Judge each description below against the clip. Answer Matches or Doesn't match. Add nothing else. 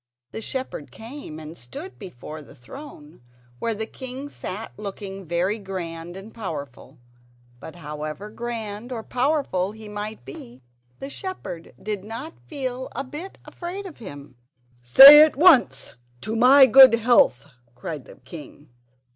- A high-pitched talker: Matches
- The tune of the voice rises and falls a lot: Matches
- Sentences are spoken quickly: Doesn't match